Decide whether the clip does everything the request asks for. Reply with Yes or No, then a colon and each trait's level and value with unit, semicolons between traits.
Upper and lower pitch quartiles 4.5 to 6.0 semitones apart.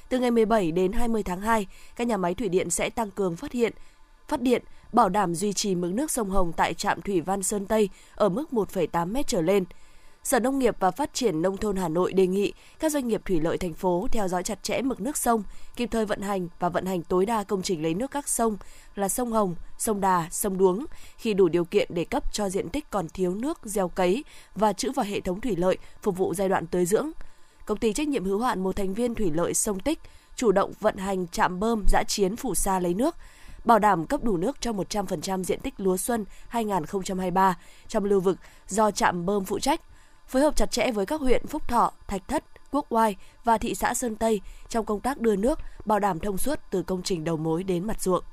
No: average, 3.9 semitones